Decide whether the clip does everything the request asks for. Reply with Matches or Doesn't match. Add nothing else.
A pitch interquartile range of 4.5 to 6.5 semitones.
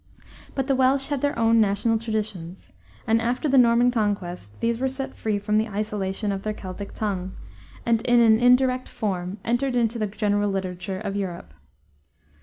Doesn't match